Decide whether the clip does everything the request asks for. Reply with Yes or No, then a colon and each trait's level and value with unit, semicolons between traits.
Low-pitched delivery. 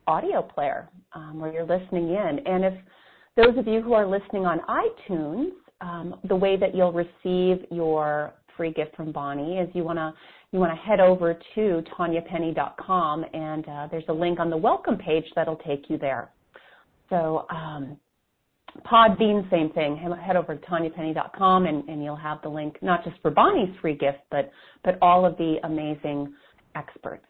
No: medium, 170 Hz